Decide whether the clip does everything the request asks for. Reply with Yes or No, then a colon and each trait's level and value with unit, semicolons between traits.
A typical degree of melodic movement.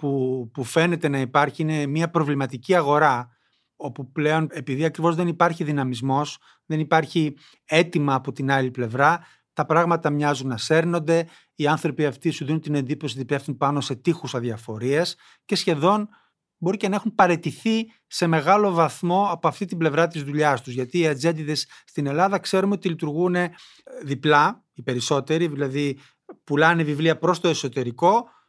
Yes: average, 3.2 semitones